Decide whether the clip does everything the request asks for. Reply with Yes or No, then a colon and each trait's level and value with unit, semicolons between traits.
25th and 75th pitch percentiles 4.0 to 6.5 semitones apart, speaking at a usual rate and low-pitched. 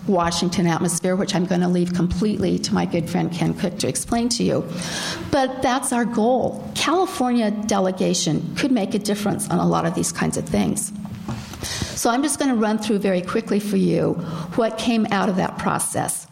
No: average, 4.8 semitones; average, 195 wpm; high, 200 Hz